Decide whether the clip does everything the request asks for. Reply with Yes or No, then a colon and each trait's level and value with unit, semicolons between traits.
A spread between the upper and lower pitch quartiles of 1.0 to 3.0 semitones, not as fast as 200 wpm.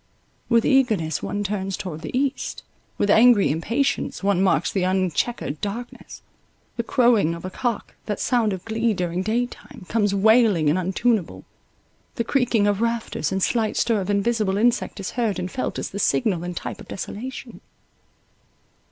No: average, 3.9 semitones; average, 160 wpm